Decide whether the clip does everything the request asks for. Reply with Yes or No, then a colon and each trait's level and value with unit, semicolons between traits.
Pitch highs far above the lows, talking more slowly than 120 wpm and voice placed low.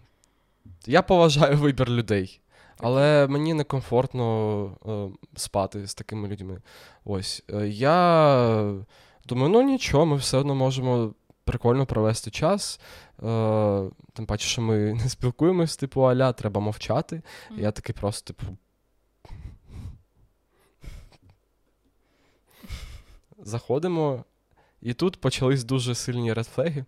No: average, 4.8 semitones; slow, 105 wpm; low, 120 Hz